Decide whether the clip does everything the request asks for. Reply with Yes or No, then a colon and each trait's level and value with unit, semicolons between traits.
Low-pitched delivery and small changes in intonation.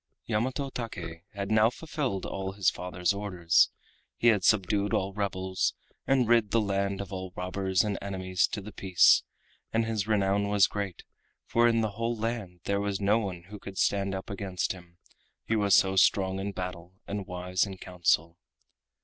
Yes: low, 100 Hz; narrow, 2.3 semitones